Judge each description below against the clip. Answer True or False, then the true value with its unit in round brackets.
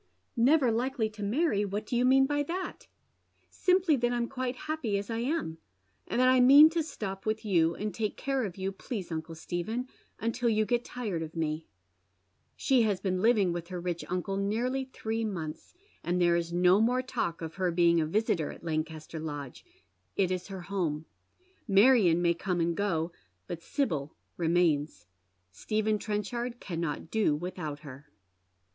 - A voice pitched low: False (200 Hz)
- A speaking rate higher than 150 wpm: True (180 wpm)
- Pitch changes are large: True (6.1 semitones)